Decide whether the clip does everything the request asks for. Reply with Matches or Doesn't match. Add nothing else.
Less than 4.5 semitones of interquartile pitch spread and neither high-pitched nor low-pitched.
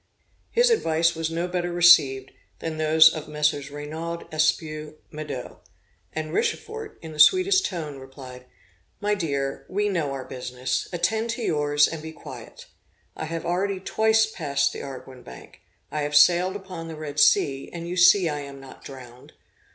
Matches